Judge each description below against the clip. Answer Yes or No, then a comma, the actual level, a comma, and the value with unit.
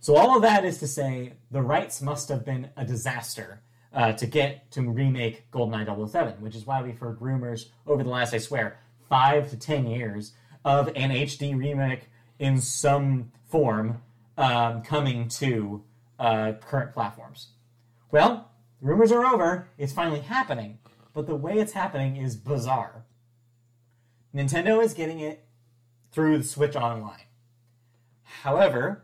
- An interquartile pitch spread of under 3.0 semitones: No, average, 3.5 semitones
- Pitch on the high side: No, low, 120 Hz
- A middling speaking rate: Yes, average, 150 wpm